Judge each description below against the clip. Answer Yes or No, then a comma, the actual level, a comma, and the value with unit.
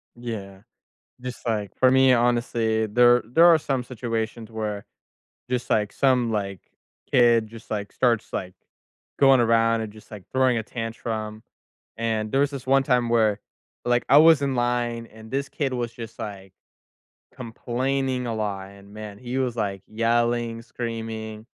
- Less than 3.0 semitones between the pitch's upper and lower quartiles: Yes, narrow, 2.4 semitones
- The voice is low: Yes, low, 115 Hz